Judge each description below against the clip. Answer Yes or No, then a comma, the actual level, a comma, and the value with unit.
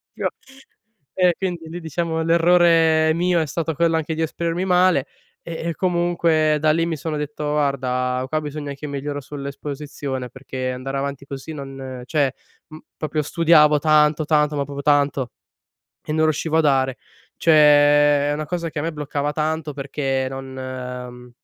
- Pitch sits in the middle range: Yes, medium, 150 Hz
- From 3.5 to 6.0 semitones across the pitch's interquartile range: No, average, 2.7 semitones